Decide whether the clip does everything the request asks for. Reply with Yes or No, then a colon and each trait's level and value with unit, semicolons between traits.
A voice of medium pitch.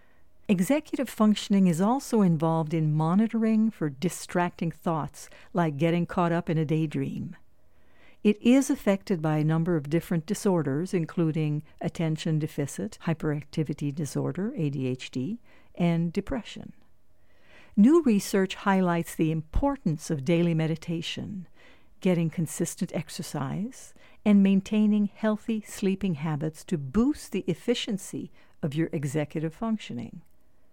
Yes: medium, 175 Hz